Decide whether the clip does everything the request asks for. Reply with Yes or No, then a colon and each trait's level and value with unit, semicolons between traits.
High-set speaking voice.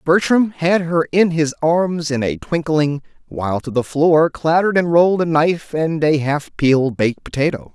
No: medium, 155 Hz